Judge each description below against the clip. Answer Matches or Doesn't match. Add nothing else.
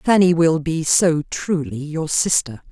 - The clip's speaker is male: Doesn't match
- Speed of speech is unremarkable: Matches